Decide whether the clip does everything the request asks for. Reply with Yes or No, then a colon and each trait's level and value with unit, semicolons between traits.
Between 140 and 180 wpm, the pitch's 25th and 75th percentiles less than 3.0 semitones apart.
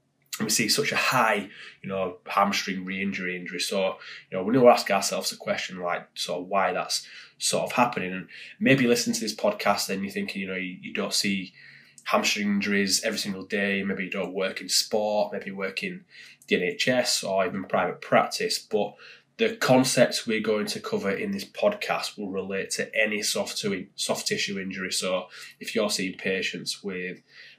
No: average, 200 wpm; narrow, 2.5 semitones